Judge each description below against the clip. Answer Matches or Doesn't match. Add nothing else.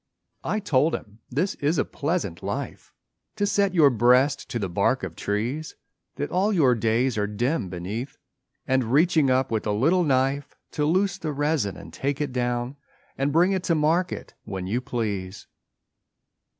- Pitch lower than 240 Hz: Matches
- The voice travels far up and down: Matches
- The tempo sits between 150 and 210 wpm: Matches